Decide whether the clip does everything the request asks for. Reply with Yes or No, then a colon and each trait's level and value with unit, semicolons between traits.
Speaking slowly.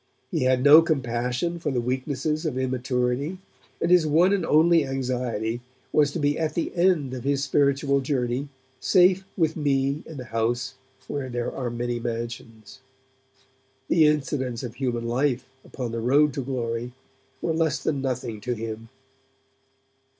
No: average, 155 wpm